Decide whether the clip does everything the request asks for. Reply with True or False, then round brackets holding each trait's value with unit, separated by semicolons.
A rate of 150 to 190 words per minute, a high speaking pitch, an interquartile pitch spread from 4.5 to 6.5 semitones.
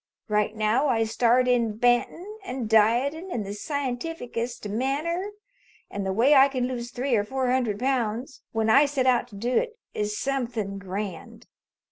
False (170 wpm; 245 Hz; 3.8 semitones)